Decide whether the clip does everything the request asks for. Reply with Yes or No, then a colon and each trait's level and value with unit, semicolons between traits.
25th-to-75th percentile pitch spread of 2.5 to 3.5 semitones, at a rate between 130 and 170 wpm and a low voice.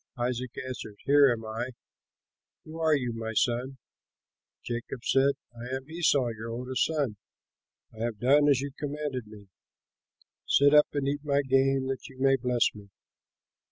Yes: average, 3.1 semitones; average, 160 wpm; low, 130 Hz